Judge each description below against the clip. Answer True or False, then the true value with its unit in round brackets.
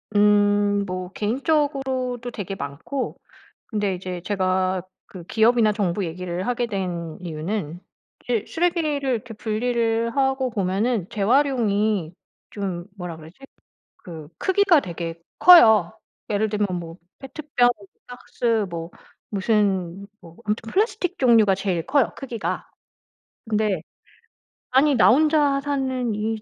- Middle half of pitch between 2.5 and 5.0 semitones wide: False (5.4 semitones)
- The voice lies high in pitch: True (215 Hz)